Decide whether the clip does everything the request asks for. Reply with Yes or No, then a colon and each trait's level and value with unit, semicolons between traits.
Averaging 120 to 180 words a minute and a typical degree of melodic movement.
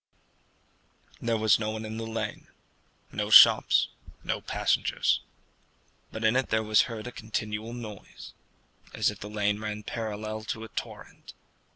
No: average, 150 wpm; narrow, 1.0 semitones